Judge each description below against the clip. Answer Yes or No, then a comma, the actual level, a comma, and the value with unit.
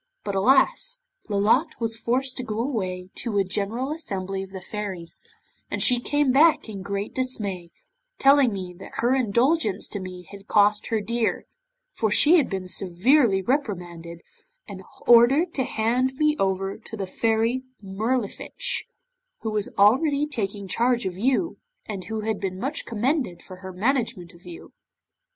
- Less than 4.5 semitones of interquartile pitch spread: No, average, 5.0 semitones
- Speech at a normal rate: Yes, average, 160 wpm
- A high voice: Yes, high, 220 Hz